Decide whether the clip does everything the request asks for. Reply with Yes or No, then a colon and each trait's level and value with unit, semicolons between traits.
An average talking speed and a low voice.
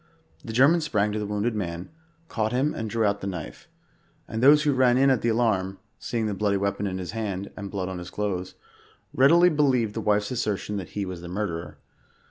No: fast, 220 wpm; low, 105 Hz